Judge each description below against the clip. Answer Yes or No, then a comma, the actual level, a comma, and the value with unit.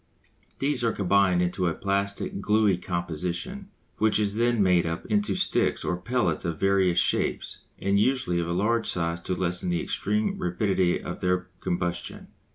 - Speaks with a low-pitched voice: Yes, very low, 95 Hz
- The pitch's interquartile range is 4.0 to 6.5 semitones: No, average, 3.2 semitones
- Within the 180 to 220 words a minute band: No, average, 160 wpm